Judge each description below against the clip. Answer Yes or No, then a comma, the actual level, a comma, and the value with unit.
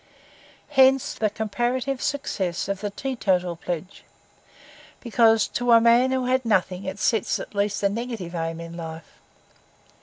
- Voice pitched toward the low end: No, high, 215 Hz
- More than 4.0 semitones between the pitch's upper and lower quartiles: Yes, average, 5.1 semitones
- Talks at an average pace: Yes, average, 145 wpm